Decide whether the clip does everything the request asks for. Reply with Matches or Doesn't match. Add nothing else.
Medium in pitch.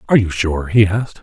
Doesn't match